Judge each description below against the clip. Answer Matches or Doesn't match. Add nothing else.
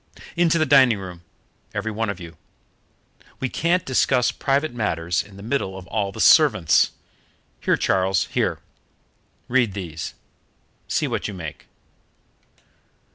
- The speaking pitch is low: Matches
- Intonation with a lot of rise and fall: Matches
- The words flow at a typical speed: Doesn't match